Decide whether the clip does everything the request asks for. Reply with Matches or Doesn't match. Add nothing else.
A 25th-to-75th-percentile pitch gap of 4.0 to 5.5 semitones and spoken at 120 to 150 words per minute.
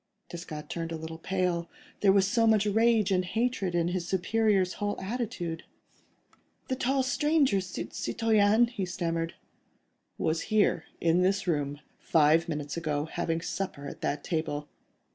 Matches